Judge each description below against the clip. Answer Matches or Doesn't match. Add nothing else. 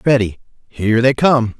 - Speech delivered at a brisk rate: Doesn't match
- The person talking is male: Matches